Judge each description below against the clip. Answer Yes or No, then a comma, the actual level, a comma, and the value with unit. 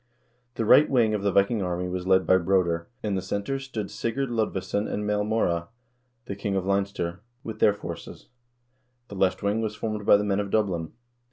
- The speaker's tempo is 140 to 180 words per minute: No, average, 190 wpm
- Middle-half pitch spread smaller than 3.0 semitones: Yes, narrow, 2.6 semitones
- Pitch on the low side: Yes, low, 100 Hz